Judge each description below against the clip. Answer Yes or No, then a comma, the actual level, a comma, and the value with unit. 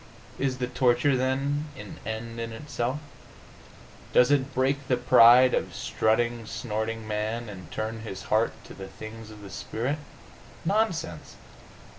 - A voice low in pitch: Yes, low, 120 Hz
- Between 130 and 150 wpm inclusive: Yes, average, 140 wpm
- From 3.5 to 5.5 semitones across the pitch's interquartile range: No, average, 3.1 semitones